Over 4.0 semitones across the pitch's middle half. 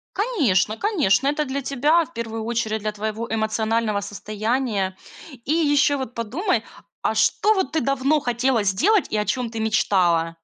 Yes: average, 5.1 semitones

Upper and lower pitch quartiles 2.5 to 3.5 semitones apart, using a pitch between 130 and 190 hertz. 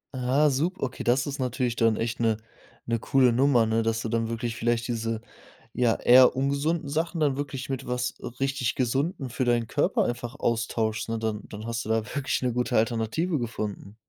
No: average, 2.9 semitones; low, 120 Hz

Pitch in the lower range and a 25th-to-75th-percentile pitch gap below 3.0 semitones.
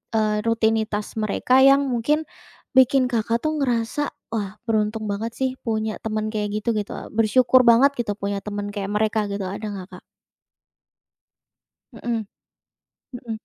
No: high, 220 Hz; narrow, 2.4 semitones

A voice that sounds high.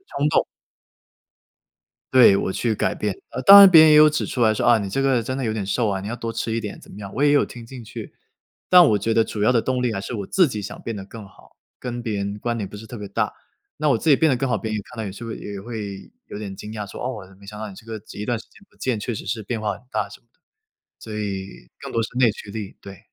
No: low, 110 Hz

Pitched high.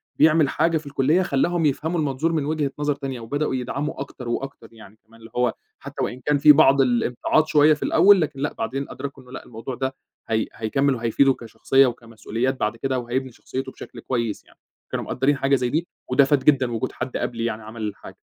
No: low, 135 Hz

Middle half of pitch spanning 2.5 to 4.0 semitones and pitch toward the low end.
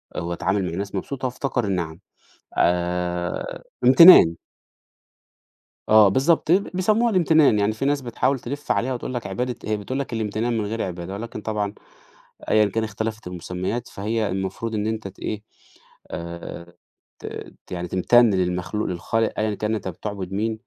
No: average, 4.6 semitones; low, 105 Hz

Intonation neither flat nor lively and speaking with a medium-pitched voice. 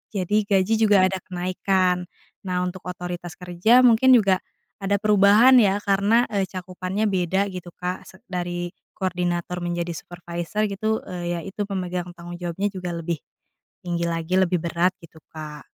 No: narrow, 2.2 semitones; medium, 180 Hz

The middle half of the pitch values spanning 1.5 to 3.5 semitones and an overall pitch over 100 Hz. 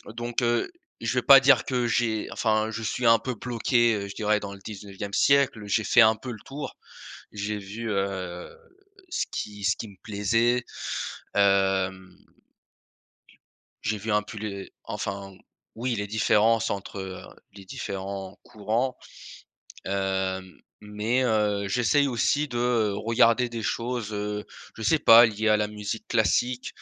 Yes: average, 3.0 semitones; low, 110 Hz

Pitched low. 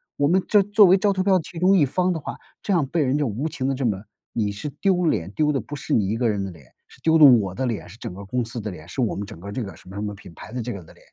Yes: low, 125 Hz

